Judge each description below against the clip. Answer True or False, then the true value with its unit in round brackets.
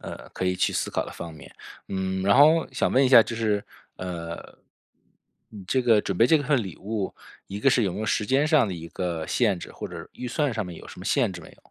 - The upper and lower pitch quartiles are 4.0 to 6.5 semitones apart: True (5.4 semitones)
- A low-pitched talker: True (105 Hz)